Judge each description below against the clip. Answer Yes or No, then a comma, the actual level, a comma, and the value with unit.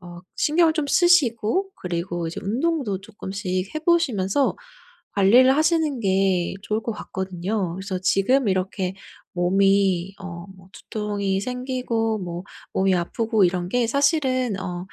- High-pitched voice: Yes, high, 200 Hz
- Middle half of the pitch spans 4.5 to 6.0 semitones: Yes, wide, 5.4 semitones